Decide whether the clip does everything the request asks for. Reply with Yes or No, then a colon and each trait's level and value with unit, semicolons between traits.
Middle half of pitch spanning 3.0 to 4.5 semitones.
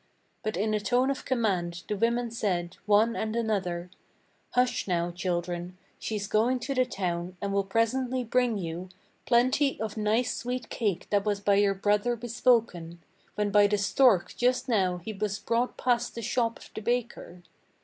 Yes: average, 4.1 semitones